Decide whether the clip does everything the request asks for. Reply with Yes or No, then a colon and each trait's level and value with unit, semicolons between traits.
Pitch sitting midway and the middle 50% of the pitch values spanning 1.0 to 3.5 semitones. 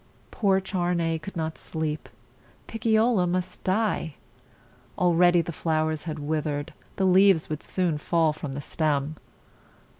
Yes: medium, 165 Hz; average, 3.1 semitones